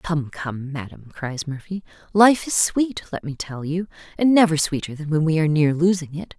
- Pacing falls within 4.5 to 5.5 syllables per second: Yes, 5.0 syllables/s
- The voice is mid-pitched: Yes, medium, 160 Hz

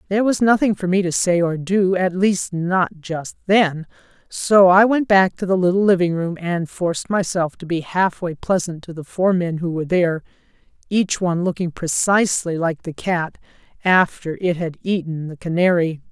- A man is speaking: No, female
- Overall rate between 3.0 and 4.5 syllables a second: No, 4.9 syllables/s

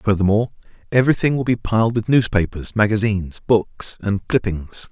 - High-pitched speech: No, low, 105 Hz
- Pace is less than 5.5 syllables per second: No, 5.6 syllables/s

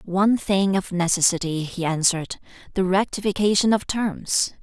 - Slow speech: Yes, slow, 115 wpm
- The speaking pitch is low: No, high, 190 Hz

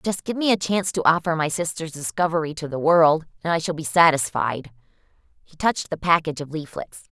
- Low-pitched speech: No, medium, 160 Hz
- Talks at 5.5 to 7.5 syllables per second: Yes, 5.8 syllables/s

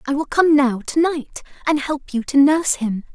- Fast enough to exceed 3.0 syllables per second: Yes, 5.0 syllables/s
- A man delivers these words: No, female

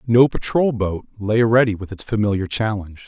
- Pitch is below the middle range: Yes, low, 110 Hz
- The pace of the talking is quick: No, average, 175 wpm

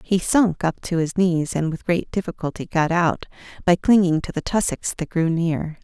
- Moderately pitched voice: Yes, medium, 170 Hz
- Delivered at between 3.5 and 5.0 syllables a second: Yes, 4.9 syllables/s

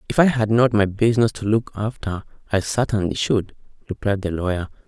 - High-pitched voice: No, low, 105 Hz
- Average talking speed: Yes, average, 185 wpm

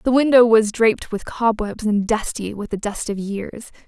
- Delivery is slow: No, average, 200 wpm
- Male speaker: No, female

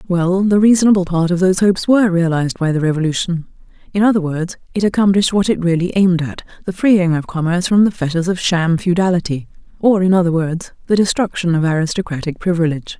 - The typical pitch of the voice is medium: Yes, medium, 180 Hz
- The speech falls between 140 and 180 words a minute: No, average, 190 wpm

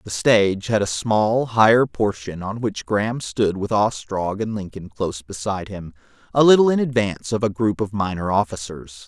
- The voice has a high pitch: No, low, 105 Hz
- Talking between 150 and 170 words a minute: No, average, 185 wpm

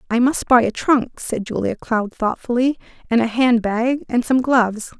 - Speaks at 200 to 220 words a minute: No, average, 190 wpm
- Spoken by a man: No, female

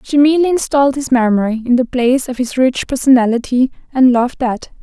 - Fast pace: No, average, 185 wpm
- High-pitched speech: Yes, very high, 255 Hz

